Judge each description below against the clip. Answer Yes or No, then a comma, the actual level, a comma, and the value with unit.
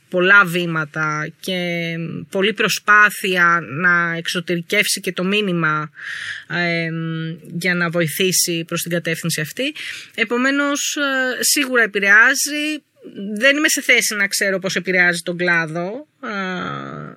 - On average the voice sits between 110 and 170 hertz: No, medium, 180 Hz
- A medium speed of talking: No, slow, 110 wpm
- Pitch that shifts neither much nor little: Yes, average, 3.9 semitones